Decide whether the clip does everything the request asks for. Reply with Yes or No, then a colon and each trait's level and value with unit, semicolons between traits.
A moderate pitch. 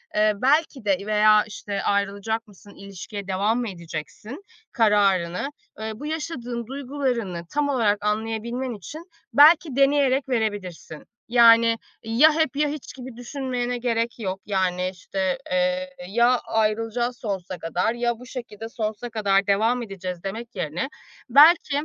No: high, 225 Hz